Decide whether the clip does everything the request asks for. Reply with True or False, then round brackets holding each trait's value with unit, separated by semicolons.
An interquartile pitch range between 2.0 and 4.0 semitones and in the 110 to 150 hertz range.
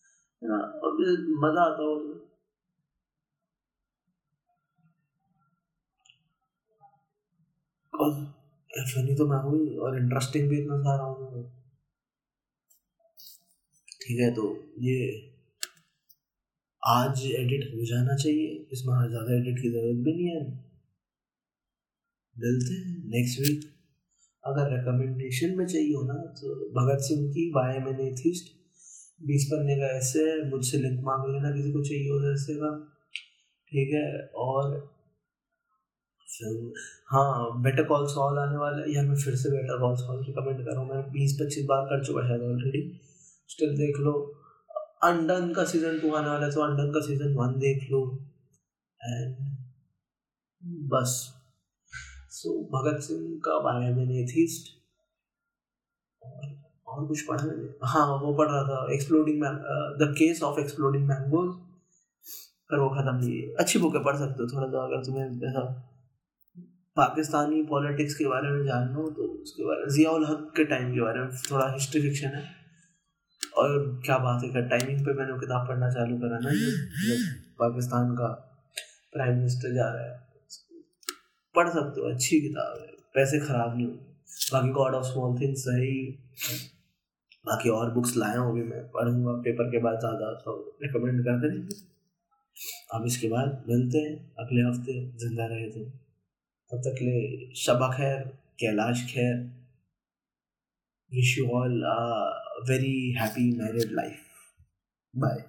True (3.5 semitones; 140 Hz)